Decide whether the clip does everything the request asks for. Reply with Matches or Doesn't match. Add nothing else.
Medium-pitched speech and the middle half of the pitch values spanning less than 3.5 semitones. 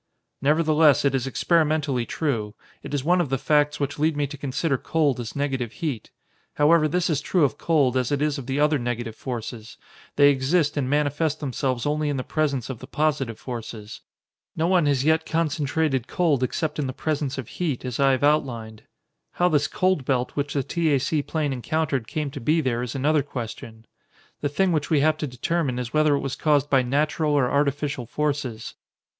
Matches